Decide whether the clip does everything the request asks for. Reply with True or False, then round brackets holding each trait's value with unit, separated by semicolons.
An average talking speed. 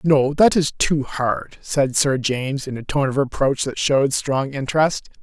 True (195 wpm)